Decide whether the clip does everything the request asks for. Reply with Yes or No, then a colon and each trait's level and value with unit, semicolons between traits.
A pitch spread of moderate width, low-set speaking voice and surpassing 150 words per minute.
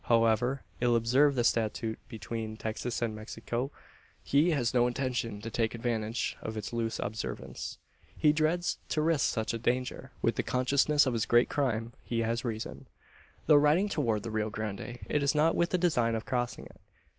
Yes: average, 3.8 semitones; low, 120 Hz; average, 180 wpm